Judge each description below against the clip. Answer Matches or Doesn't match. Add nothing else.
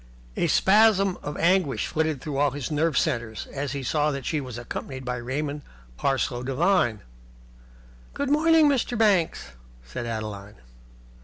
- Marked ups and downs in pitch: Matches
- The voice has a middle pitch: Matches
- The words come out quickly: Doesn't match